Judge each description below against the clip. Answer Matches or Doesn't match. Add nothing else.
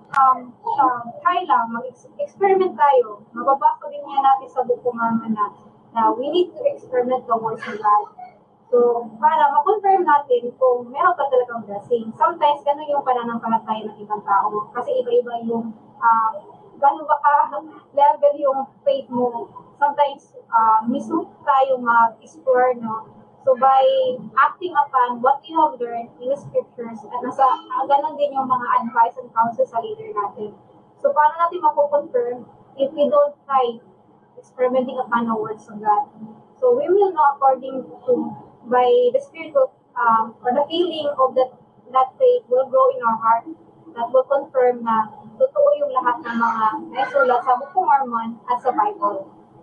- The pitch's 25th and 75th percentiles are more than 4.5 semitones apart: Doesn't match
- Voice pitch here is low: Doesn't match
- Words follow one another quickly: Matches